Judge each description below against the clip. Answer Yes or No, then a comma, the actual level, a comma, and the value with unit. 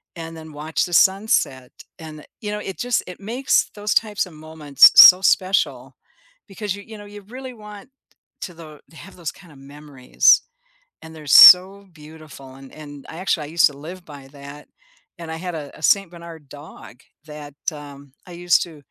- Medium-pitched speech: Yes, medium, 160 Hz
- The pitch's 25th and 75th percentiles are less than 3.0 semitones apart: No, average, 4.7 semitones